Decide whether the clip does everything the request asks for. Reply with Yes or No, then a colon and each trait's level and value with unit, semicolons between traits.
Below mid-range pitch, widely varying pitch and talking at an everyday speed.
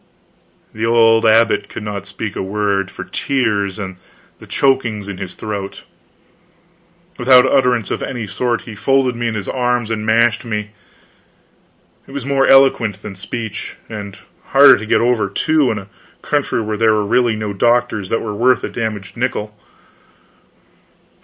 No: low, 110 Hz; average, 2.9 semitones; average, 160 wpm